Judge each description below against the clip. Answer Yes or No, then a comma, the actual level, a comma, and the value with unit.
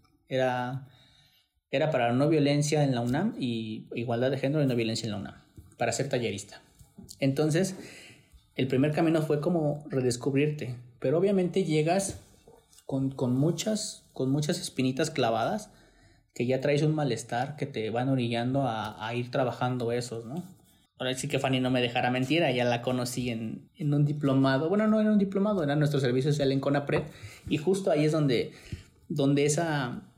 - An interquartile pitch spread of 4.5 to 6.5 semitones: No, average, 3.5 semitones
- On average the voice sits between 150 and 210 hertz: No, low, 135 Hz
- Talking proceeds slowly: No, average, 170 wpm